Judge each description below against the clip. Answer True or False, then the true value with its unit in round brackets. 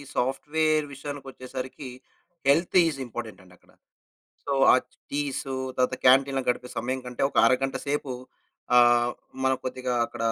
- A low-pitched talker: True (130 Hz)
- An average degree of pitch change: False (2.1 semitones)